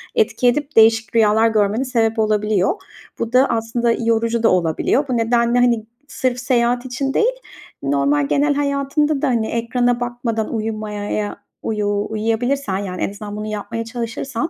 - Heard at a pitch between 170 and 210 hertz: No, high, 230 Hz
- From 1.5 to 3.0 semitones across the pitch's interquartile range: Yes, narrow, 2.6 semitones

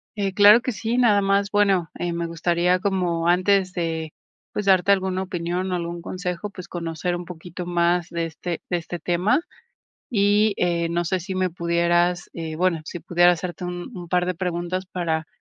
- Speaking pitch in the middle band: Yes, medium, 180 Hz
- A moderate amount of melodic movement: No, narrow, 1.8 semitones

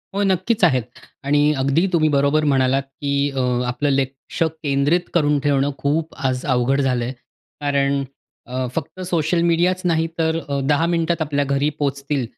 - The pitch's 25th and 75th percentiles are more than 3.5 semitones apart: No, average, 3.0 semitones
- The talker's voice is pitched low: No, medium, 145 Hz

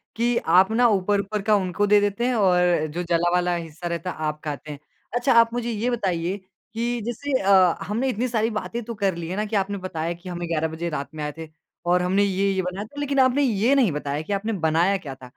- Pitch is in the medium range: No, high, 195 Hz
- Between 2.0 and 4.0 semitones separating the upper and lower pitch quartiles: No, average, 4.7 semitones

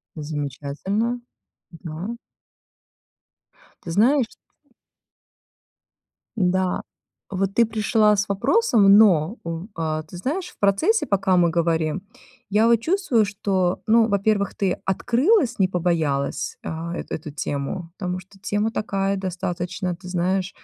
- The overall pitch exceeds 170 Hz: Yes, high, 190 Hz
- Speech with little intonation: No, average, 4.1 semitones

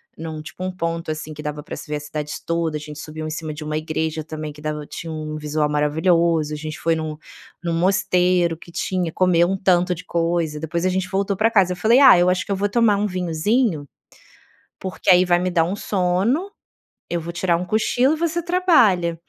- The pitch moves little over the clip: No, average, 3.2 semitones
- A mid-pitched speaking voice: Yes, medium, 170 Hz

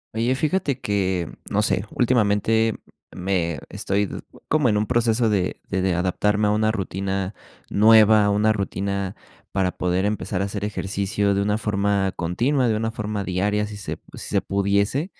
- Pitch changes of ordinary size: No, narrow, 2.1 semitones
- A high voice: No, low, 105 Hz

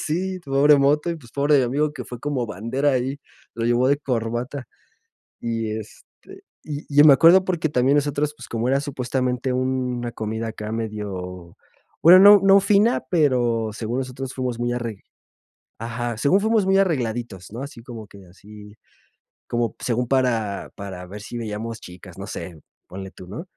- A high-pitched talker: No, low, 125 Hz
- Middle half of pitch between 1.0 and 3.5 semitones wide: No, average, 4.3 semitones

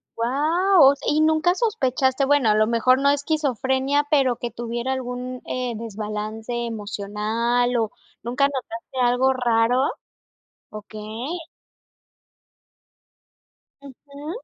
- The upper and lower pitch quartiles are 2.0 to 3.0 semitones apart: No, average, 3.5 semitones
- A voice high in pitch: Yes, very high, 250 Hz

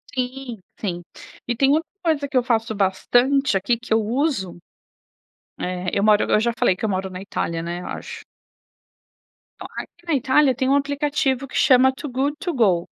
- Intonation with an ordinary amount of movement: No, wide, 5.8 semitones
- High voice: Yes, high, 245 Hz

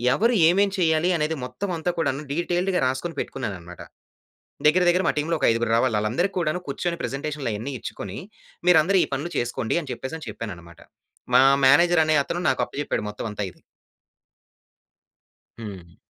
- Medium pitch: Yes, medium, 150 Hz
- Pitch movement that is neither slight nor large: No, wide, 7.2 semitones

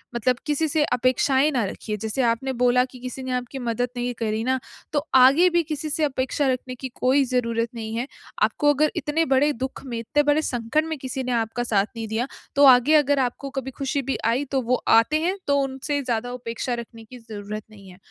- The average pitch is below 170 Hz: No, very high, 255 Hz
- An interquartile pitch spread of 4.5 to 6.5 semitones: No, average, 3.3 semitones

